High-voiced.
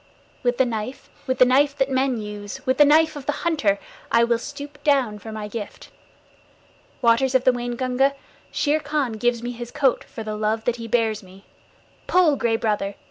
Yes: high, 245 Hz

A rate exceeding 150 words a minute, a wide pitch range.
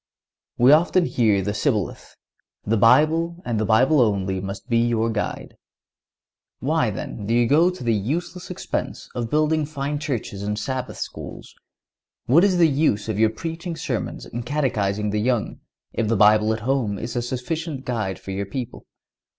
Yes: average, 170 wpm; wide, 6.1 semitones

